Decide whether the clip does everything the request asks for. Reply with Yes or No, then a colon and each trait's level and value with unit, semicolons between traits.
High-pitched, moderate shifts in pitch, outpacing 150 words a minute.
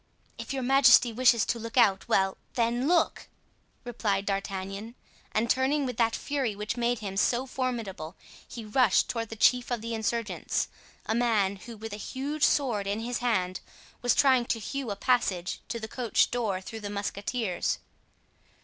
Yes: high, 230 Hz; average, 3.3 semitones; average, 165 wpm